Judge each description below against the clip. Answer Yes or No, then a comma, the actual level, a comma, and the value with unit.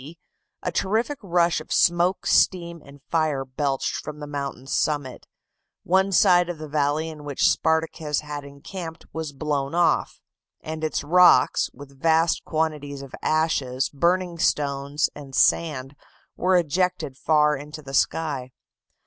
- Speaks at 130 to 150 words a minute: Yes, average, 140 wpm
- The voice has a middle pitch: Yes, medium, 155 Hz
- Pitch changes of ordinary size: Yes, average, 3.2 semitones